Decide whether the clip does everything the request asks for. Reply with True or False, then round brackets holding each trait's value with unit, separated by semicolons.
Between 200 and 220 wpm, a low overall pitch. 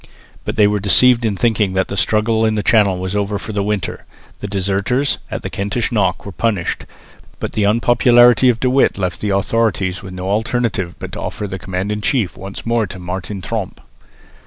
True (205 wpm; 105 Hz)